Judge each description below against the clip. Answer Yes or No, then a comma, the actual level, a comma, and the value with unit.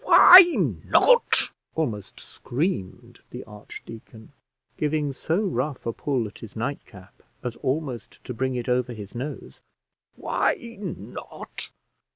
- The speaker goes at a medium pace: No, slow, 120 wpm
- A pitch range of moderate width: Yes, average, 4.7 semitones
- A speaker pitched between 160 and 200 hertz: No, low, 125 Hz